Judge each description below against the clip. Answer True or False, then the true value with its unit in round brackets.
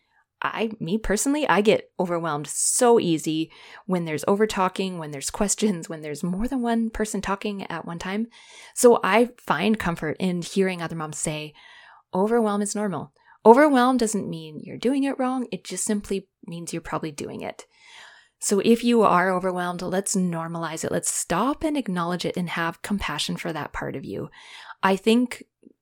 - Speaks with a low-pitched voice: False (195 Hz)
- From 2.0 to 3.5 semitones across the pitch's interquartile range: False (5.0 semitones)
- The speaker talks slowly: False (175 wpm)